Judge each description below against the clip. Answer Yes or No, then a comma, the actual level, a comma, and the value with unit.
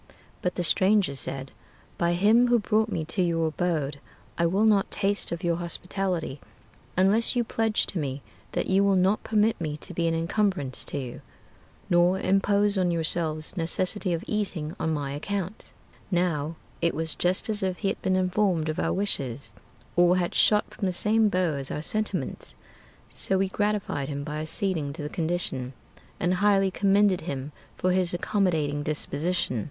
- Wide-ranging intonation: No, average, 4.1 semitones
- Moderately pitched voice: Yes, medium, 180 Hz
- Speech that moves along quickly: No, average, 175 wpm